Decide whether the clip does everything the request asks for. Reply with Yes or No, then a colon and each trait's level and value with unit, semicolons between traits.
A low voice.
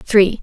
No: high, 200 Hz